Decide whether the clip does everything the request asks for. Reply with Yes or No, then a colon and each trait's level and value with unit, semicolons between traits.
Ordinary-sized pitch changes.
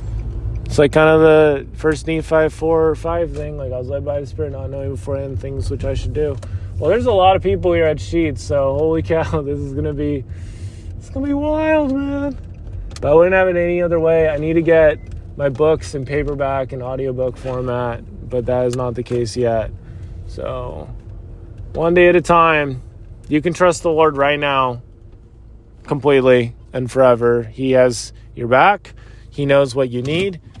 No: wide, 6.0 semitones